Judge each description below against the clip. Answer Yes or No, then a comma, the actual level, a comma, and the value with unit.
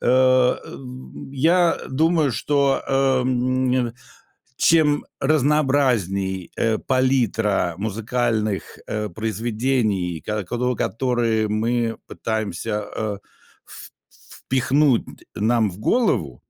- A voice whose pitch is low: Yes, low, 120 Hz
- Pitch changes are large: No, average, 3.6 semitones